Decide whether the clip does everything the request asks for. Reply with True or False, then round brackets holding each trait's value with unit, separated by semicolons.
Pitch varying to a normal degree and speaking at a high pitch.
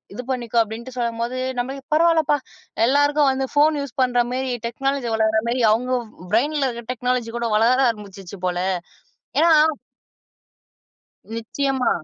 True (3.1 semitones; 250 Hz)